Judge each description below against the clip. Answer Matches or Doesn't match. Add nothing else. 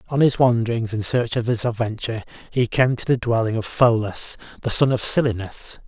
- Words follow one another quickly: Doesn't match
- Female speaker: Doesn't match